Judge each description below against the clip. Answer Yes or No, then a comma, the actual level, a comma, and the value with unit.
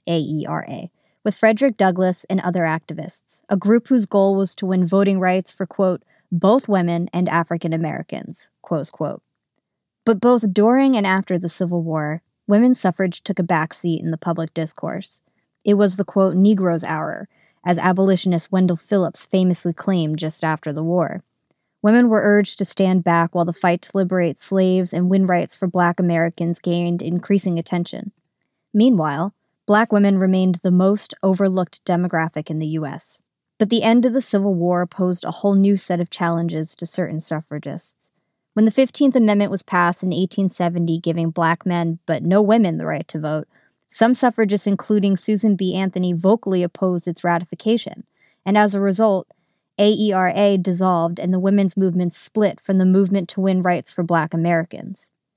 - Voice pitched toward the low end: No, medium, 185 Hz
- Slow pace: No, average, 170 wpm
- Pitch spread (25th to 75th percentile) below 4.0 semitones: Yes, average, 2.8 semitones